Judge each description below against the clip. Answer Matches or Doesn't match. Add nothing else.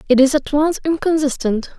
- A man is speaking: Doesn't match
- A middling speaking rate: Matches